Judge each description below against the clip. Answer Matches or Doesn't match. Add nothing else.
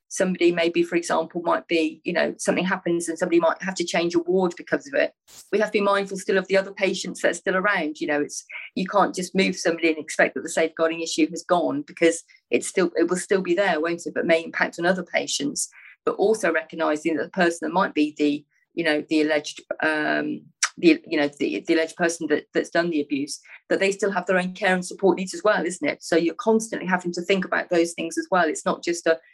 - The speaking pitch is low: Doesn't match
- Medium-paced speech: Doesn't match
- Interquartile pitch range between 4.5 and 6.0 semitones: Doesn't match